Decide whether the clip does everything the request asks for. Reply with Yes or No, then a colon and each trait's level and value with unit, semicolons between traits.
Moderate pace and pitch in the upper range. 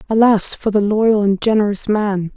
Yes: average, 180 wpm; high, 210 Hz